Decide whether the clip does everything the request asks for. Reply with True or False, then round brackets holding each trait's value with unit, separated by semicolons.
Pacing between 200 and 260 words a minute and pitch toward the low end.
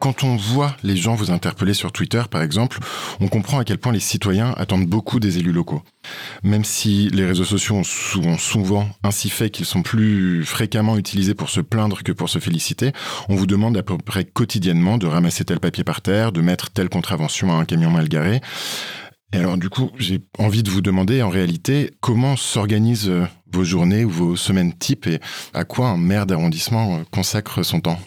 True (205 wpm; 100 Hz)